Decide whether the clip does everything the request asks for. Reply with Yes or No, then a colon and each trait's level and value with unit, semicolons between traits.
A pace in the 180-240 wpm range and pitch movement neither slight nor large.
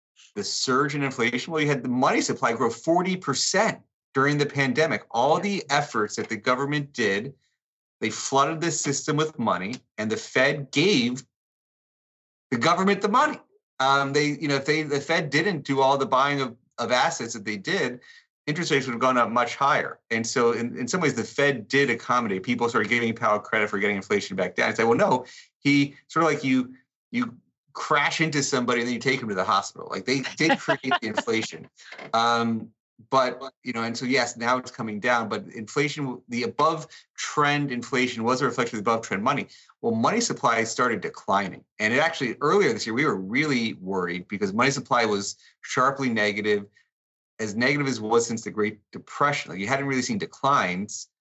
Yes: average, 200 wpm; average, 4.0 semitones